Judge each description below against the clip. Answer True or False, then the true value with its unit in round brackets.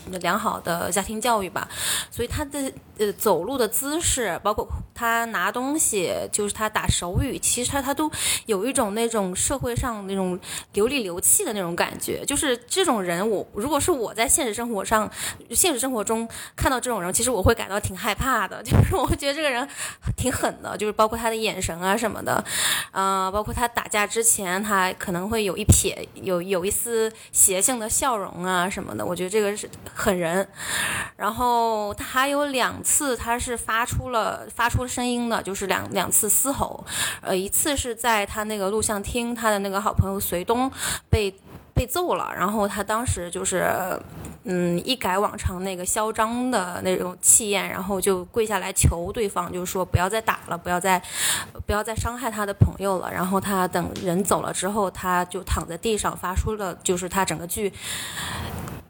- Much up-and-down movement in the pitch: False (3.9 semitones)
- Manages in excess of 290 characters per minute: False (275 characters per minute)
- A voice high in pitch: True (210 Hz)